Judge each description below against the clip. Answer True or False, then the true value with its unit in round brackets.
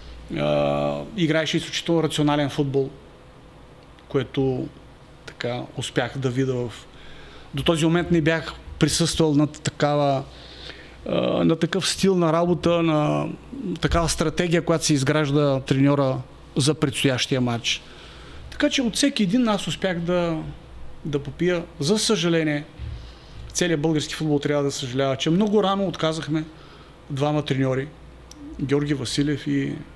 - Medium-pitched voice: True (150 Hz)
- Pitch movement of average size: True (3.4 semitones)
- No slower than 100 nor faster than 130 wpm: True (120 wpm)